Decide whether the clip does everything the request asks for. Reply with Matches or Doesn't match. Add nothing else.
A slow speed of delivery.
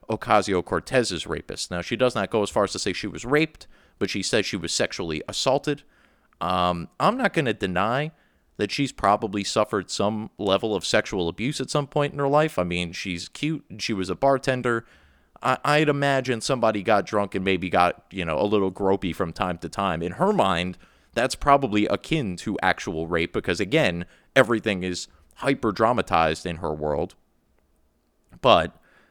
Doesn't match